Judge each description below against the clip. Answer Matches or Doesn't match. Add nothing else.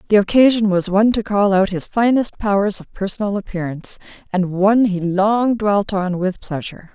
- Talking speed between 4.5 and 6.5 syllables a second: Matches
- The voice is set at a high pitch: Matches